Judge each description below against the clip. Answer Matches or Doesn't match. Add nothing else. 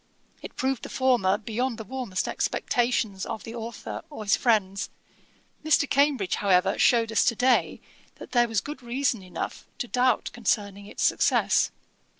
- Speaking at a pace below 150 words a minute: Doesn't match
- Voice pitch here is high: Matches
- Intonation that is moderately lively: Matches